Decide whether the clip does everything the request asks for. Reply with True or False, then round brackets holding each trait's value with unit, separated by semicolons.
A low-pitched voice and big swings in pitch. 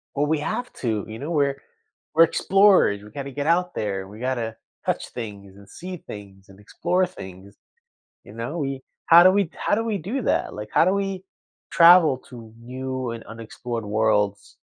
True (130 Hz; 8.4 semitones)